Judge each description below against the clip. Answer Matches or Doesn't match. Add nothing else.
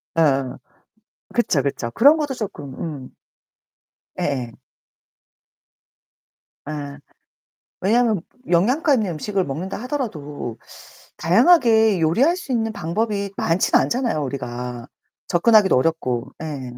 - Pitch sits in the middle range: Matches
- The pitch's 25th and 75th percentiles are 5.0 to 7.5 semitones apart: Doesn't match